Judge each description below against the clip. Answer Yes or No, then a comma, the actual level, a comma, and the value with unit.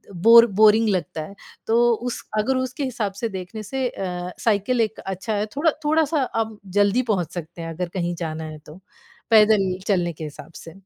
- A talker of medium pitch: No, high, 205 Hz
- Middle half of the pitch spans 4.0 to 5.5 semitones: Yes, average, 4.6 semitones